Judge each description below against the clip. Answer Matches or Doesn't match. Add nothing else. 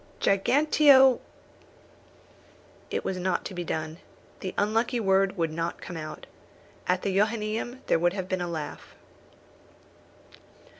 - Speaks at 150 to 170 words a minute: Doesn't match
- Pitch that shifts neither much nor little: Matches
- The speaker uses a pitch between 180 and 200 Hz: Matches